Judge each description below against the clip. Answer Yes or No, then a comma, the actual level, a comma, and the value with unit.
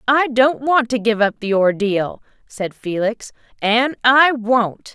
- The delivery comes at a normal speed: Yes, average, 160 wpm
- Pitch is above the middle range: Yes, high, 230 Hz